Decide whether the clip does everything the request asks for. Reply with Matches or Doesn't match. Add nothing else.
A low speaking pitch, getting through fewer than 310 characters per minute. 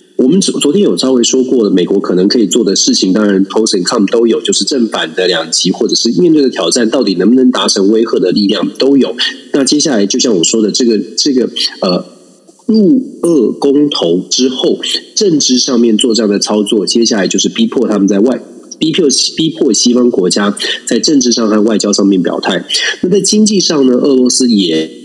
Doesn't match